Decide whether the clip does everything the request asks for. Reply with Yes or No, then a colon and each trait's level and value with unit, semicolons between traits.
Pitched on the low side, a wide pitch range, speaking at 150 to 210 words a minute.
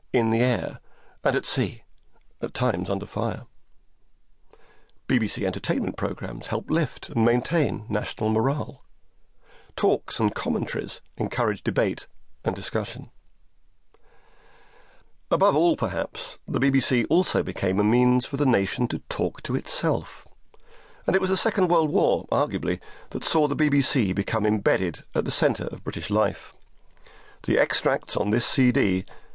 No: low, 125 Hz; wide, 6.1 semitones; slow, 135 wpm